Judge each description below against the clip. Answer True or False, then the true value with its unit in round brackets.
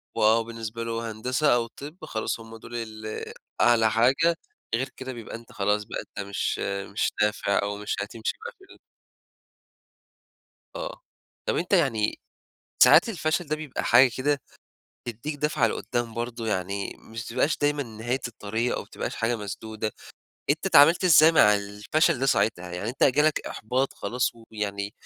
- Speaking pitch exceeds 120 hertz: False (115 Hz)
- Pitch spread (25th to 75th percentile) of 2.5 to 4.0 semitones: False (4.7 semitones)